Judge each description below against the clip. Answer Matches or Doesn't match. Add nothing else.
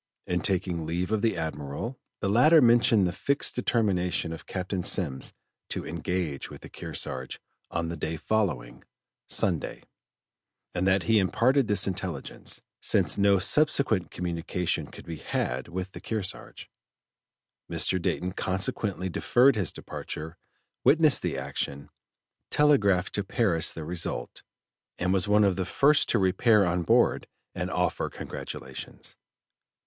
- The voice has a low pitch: Matches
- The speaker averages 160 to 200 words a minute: Doesn't match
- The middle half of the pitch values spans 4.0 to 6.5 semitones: Matches